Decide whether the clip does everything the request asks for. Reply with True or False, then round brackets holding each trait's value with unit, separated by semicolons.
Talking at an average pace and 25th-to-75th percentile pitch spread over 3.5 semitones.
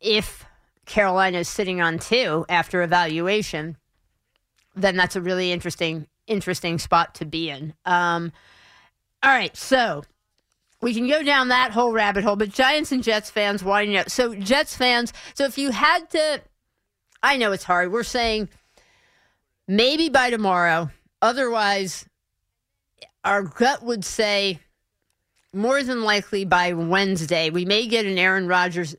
True (145 wpm; 5.1 semitones)